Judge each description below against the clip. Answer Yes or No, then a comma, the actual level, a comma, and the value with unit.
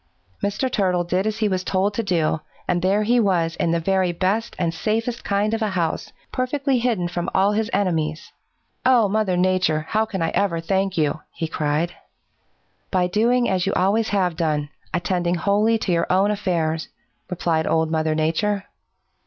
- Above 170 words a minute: Yes, average, 180 wpm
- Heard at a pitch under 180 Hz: No, medium, 185 Hz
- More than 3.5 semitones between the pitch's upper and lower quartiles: Yes, average, 3.9 semitones